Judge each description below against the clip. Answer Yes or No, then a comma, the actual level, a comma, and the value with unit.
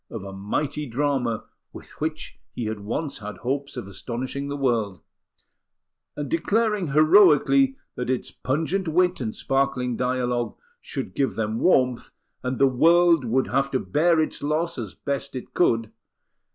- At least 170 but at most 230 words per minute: No, average, 150 wpm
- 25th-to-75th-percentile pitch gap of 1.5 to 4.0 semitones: No, average, 4.5 semitones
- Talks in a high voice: No, low, 135 Hz